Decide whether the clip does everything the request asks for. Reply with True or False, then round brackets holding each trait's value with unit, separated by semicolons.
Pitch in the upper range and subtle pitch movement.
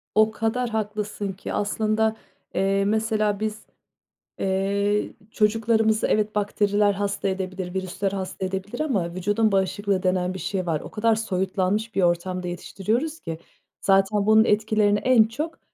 True (205 Hz; 2.3 semitones)